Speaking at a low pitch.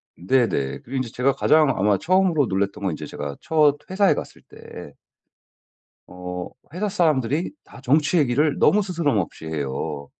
Yes: low, 130 Hz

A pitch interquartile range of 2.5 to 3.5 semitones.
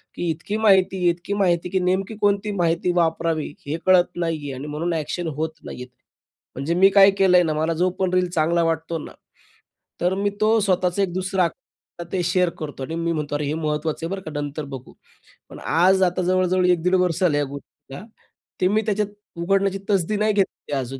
Yes: average, 3.0 semitones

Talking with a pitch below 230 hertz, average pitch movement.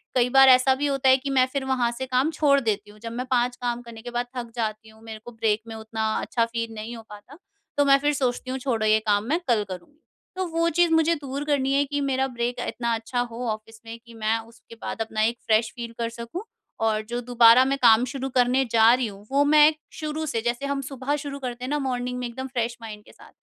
No: high, 245 Hz; average, 3.1 semitones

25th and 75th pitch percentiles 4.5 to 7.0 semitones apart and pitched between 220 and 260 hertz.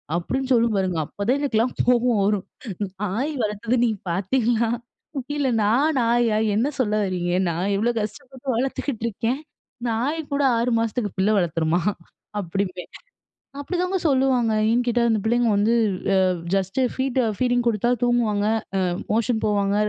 No: average, 3.7 semitones; high, 230 Hz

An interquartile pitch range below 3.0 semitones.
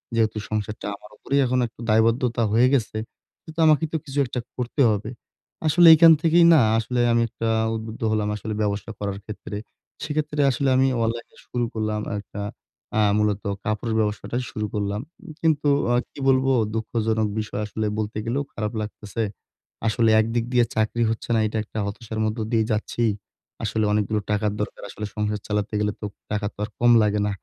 Yes: narrow, 2.4 semitones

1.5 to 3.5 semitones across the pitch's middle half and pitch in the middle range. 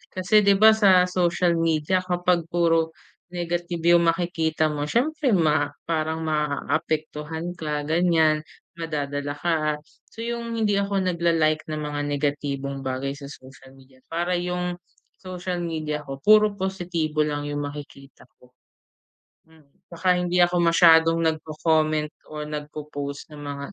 Yes: average, 3.0 semitones; medium, 160 Hz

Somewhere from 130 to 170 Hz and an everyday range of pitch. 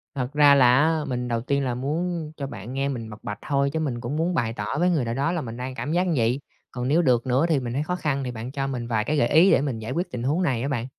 Yes: low, 135 Hz; average, 3.9 semitones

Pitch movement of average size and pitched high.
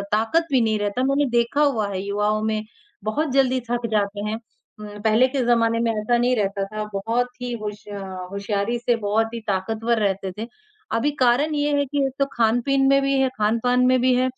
Yes: average, 3.4 semitones; high, 230 Hz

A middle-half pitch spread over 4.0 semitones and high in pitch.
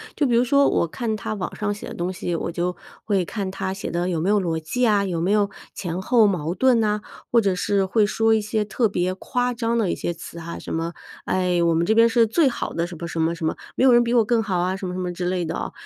Yes: average, 4.4 semitones; high, 195 Hz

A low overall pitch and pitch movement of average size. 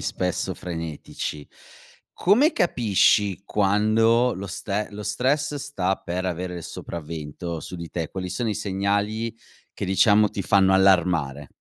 Yes: very low, 95 Hz; average, 3.5 semitones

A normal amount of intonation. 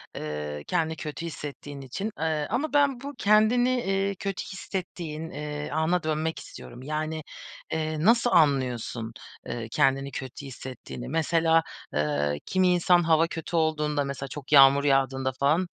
Yes: average, 4.3 semitones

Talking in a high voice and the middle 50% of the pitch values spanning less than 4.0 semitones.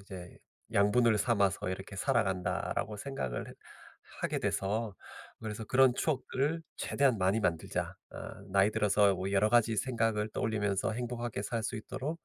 No: low, 105 Hz; average, 3.3 semitones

